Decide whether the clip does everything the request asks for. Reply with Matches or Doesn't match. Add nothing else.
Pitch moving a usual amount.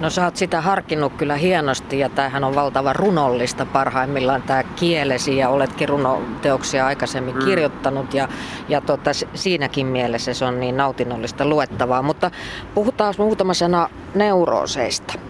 Matches